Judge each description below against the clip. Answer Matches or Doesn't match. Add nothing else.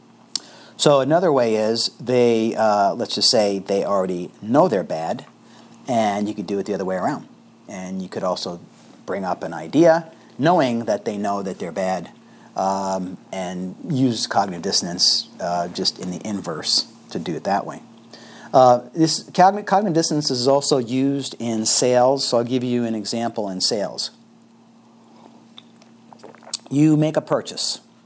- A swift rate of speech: Doesn't match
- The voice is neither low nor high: Doesn't match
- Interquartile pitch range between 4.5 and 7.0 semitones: Matches